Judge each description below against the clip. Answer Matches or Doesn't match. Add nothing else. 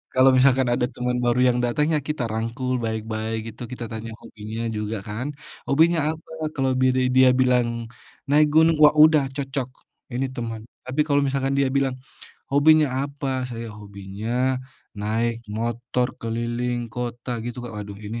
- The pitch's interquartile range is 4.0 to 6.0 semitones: Doesn't match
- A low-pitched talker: Matches